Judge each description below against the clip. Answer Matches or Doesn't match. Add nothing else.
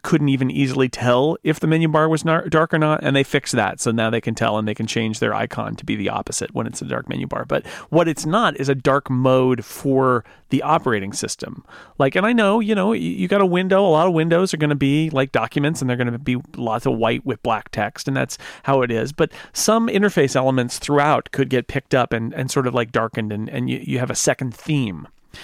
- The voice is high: Doesn't match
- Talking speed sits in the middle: Doesn't match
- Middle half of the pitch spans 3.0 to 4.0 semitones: Doesn't match